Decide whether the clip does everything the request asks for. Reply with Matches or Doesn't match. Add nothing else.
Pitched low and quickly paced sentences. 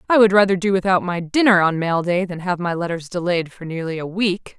Doesn't match